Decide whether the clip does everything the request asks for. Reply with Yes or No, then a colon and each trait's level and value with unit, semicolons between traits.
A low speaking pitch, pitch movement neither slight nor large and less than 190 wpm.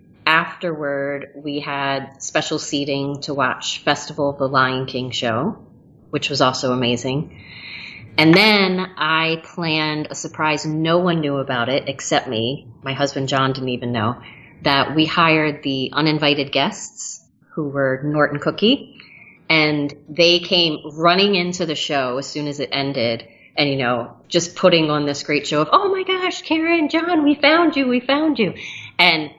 No: medium, 150 Hz; average, 3.8 semitones; average, 165 wpm